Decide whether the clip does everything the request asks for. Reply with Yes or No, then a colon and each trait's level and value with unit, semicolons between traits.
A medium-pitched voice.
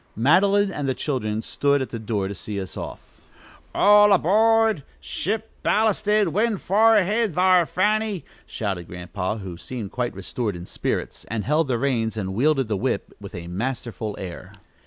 No: low, 130 Hz